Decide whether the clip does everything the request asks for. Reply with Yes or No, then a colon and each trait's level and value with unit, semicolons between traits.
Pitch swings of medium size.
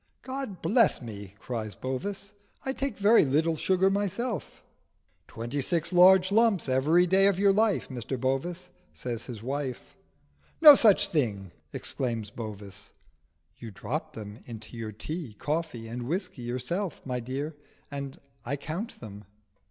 No: wide, 8.3 semitones